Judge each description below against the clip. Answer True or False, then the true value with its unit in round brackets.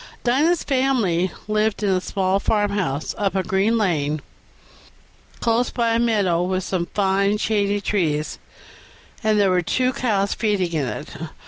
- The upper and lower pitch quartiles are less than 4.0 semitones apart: True (3.2 semitones)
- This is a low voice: False (200 Hz)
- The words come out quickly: False (140 wpm)